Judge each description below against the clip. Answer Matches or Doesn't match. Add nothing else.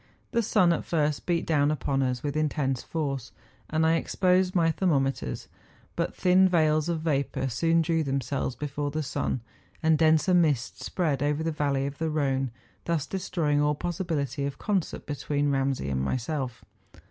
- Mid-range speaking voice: Matches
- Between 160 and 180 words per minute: Matches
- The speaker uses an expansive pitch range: Doesn't match